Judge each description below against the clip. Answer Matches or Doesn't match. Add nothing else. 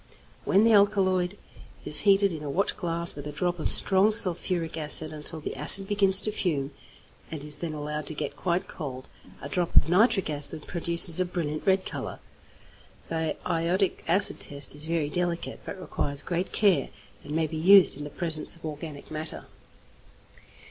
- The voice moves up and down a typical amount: Matches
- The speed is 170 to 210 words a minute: Matches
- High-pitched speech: Doesn't match